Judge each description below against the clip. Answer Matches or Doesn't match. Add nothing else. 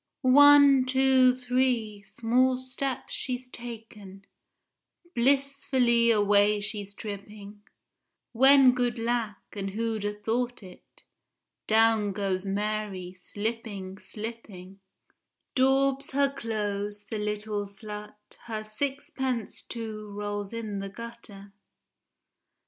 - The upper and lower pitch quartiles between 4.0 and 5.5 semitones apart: Doesn't match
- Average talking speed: Doesn't match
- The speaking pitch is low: Doesn't match